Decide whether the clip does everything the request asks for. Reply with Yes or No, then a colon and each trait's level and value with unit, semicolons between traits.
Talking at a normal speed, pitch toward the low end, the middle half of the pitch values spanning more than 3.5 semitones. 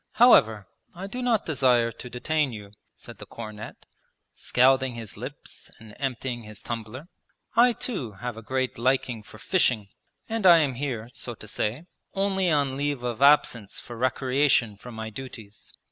Yes: average, 160 wpm; low, 125 Hz; average, 4.4 semitones